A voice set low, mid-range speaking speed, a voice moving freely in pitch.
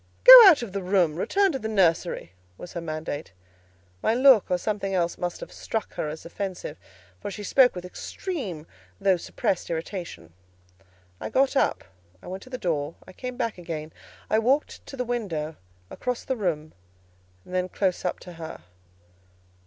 No: medium, 185 Hz; average, 170 wpm; wide, 6.2 semitones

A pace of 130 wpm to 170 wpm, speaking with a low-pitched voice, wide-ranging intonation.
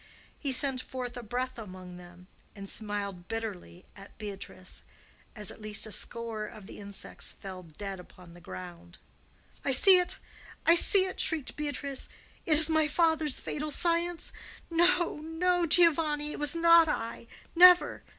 No: average, 155 wpm; very high, 255 Hz; wide, 8.3 semitones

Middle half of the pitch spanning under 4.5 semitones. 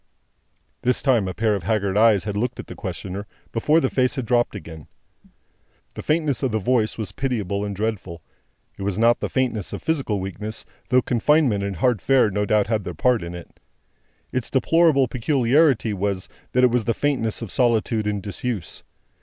Yes: average, 4.0 semitones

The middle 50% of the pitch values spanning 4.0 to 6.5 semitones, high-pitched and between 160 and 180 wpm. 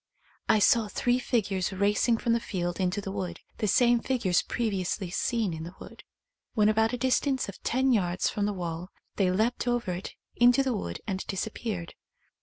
No: average, 4.4 semitones; high, 205 Hz; average, 190 wpm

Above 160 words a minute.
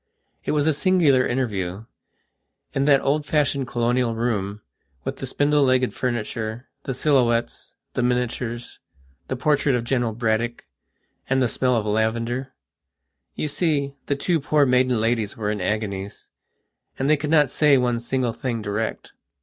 No: average, 150 wpm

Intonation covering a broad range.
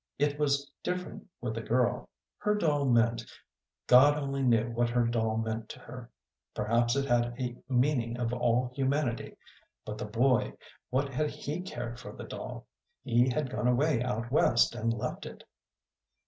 No: average, 3.0 semitones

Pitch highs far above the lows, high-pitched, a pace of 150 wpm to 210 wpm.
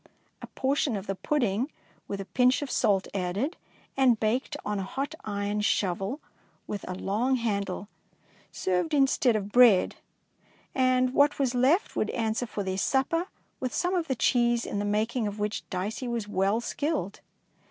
No: average, 4.6 semitones; high, 230 Hz; average, 165 wpm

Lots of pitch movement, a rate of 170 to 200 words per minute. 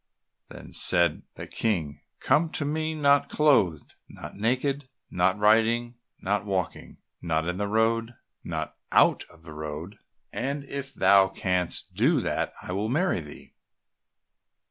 No: wide, 7.5 semitones; average, 145 wpm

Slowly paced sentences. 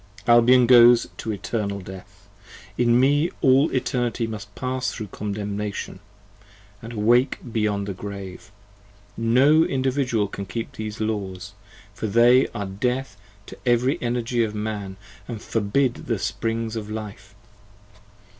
Yes: slow, 125 wpm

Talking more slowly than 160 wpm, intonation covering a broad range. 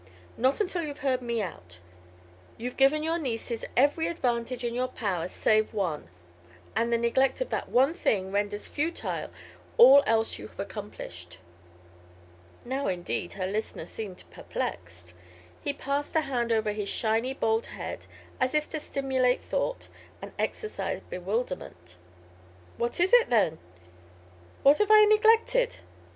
Yes: average, 140 wpm; wide, 5.8 semitones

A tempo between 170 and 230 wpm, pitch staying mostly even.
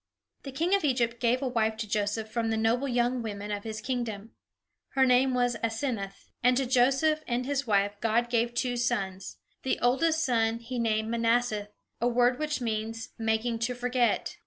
Yes: average, 185 wpm; narrow, 2.2 semitones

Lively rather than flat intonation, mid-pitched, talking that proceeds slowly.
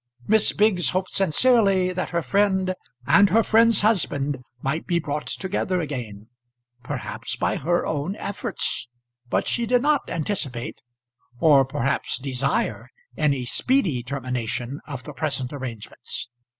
Yes: wide, 6.8 semitones; medium, 160 Hz; slow, 130 wpm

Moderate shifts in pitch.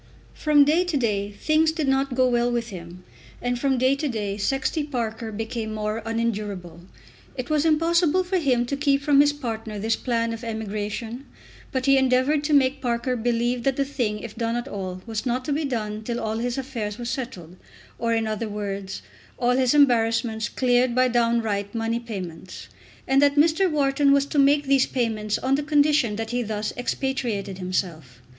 Yes: average, 4.1 semitones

